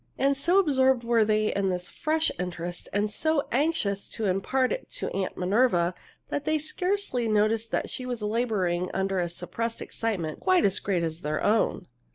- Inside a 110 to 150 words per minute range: No, average, 175 wpm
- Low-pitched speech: No, high, 220 Hz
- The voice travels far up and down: Yes, wide, 6.1 semitones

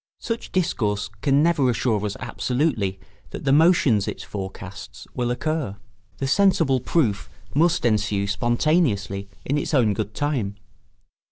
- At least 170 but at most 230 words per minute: No, slow, 135 wpm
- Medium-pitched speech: No, low, 125 Hz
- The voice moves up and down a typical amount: No, wide, 6.8 semitones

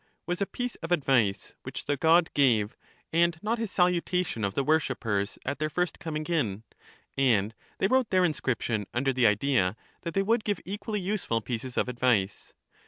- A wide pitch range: Yes, wide, 7.6 semitones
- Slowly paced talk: No, average, 185 wpm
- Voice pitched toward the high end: No, medium, 150 Hz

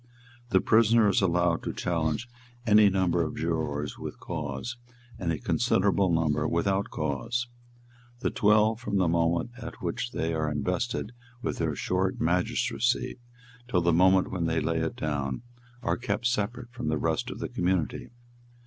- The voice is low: Yes, very low, 90 Hz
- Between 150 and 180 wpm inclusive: Yes, average, 160 wpm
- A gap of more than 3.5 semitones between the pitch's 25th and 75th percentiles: Yes, average, 4.8 semitones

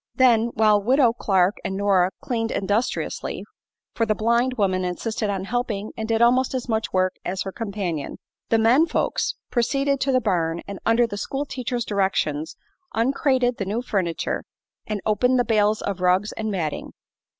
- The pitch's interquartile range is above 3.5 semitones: Yes, average, 4.0 semitones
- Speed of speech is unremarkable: Yes, average, 170 wpm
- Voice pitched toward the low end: No, high, 220 Hz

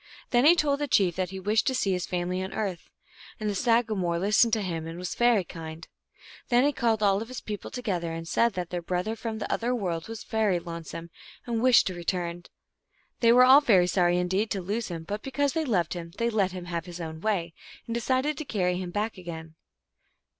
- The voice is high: Yes, high, 195 Hz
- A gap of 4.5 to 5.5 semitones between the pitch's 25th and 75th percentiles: Yes, average, 4.9 semitones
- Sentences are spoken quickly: Yes, fast, 220 wpm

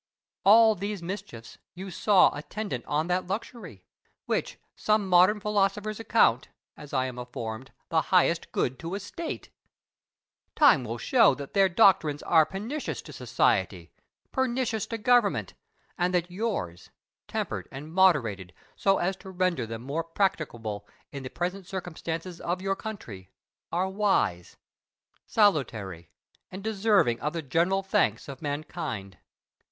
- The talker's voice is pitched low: No, medium, 180 Hz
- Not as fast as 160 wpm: Yes, slow, 135 wpm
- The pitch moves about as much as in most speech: No, wide, 6.9 semitones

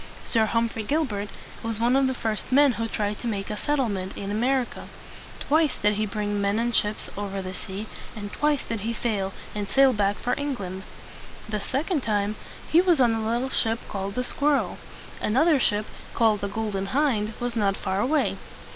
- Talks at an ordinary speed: No, fast, 210 wpm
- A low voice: No, high, 220 Hz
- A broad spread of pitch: No, average, 4.1 semitones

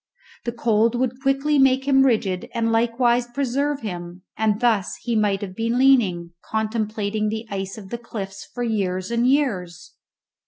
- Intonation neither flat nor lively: Yes, average, 3.6 semitones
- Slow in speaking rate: No, average, 160 wpm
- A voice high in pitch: Yes, high, 225 Hz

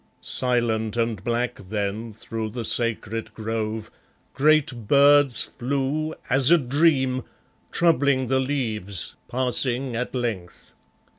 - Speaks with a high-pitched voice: No, low, 120 Hz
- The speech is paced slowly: Yes, slow, 105 wpm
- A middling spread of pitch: Yes, average, 3.4 semitones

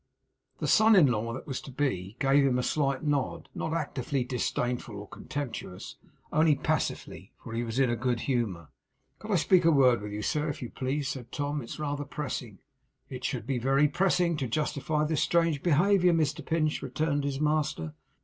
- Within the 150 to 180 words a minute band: No, average, 190 wpm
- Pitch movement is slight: No, average, 3.8 semitones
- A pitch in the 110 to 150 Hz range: Yes, medium, 140 Hz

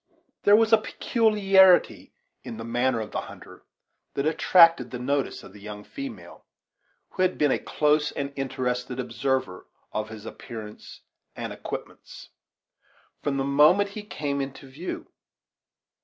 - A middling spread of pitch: No, wide, 6.7 semitones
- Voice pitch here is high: No, medium, 140 Hz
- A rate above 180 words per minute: No, average, 140 wpm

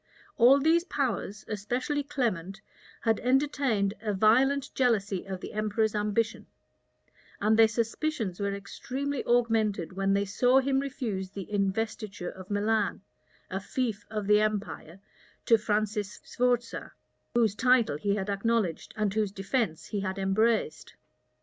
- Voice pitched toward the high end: Yes, high, 215 Hz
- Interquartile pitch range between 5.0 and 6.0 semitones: No, average, 3.5 semitones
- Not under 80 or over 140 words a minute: Yes, slow, 135 wpm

